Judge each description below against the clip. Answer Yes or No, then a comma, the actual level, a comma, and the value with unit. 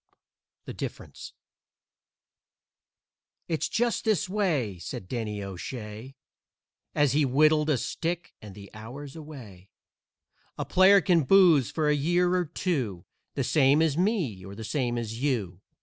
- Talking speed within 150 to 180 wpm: No, slow, 135 wpm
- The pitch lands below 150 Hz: Yes, medium, 140 Hz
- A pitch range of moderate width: No, wide, 7.5 semitones